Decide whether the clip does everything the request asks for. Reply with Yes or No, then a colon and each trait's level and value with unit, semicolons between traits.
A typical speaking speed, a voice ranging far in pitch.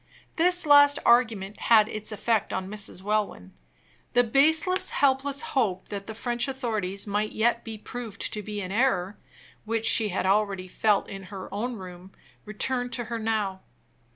No: average, 160 wpm; average, 3.6 semitones